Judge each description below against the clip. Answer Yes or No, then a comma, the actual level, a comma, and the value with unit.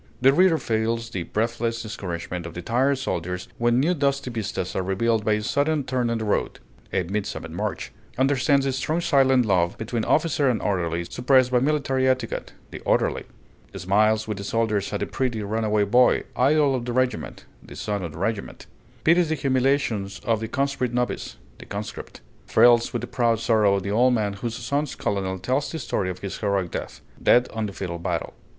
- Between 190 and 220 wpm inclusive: Yes, average, 195 wpm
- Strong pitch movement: No, average, 4.4 semitones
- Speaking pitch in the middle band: No, low, 115 Hz